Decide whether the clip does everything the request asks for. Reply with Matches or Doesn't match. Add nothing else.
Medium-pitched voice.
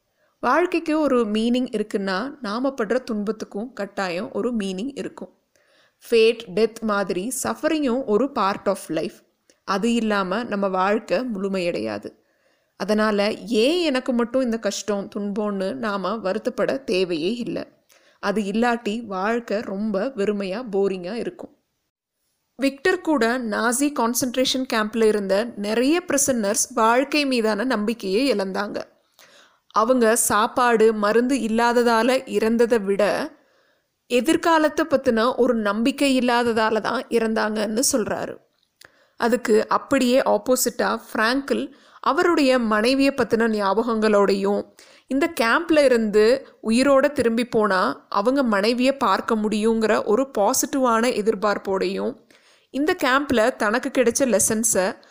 Doesn't match